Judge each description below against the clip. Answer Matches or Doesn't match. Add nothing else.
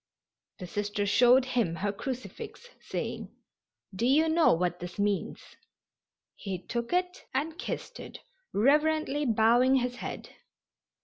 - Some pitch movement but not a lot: Doesn't match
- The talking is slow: Matches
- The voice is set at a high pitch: Matches